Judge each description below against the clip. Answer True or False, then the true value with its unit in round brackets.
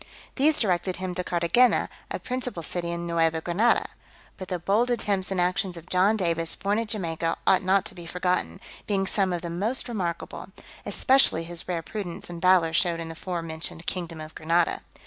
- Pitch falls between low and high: True (180 Hz)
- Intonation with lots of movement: False (2.8 semitones)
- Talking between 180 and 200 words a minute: True (190 wpm)